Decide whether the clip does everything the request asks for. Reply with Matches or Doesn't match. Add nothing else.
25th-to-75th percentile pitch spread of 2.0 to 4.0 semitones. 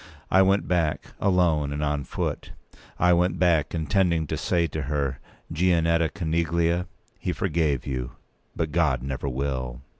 Matches